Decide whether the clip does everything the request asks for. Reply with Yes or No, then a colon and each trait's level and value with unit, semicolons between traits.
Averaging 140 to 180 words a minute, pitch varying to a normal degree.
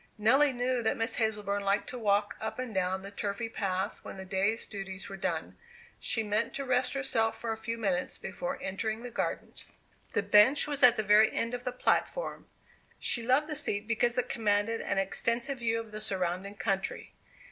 No: average, 195 wpm; average, 3.4 semitones